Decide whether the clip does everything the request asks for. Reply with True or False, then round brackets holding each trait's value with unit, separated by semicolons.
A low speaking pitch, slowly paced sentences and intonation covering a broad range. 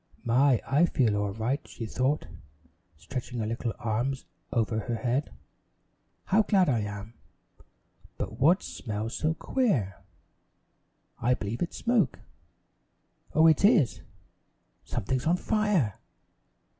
True (125 Hz; 120 wpm; 6.3 semitones)